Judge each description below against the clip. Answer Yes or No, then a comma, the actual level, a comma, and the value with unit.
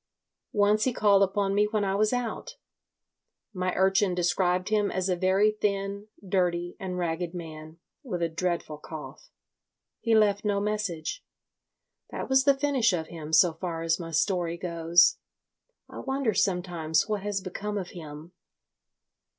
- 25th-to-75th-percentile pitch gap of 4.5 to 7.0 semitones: No, average, 3.4 semitones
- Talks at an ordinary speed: Yes, average, 150 wpm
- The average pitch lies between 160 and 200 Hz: Yes, high, 190 Hz